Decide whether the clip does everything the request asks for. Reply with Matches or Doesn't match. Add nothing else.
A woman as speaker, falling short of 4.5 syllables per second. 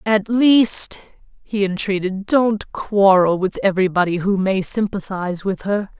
Matches